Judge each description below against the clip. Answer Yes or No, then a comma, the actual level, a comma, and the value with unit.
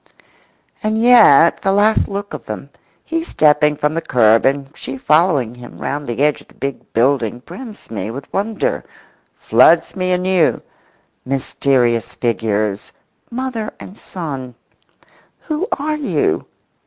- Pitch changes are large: Yes, wide, 8.2 semitones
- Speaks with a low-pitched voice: No, medium, 150 Hz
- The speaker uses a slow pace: Yes, slow, 130 wpm